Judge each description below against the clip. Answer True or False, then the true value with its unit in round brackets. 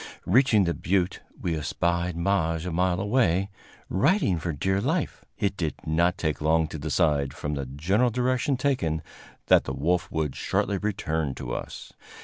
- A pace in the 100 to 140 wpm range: False (160 wpm)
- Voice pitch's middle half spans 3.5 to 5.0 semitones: True (4.0 semitones)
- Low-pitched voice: True (85 Hz)